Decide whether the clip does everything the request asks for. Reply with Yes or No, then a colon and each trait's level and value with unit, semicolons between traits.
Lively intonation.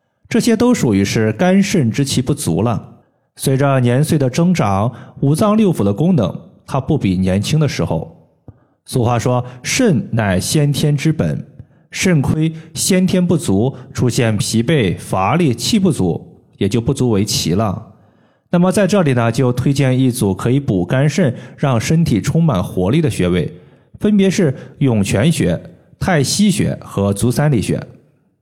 Yes: wide, 5.7 semitones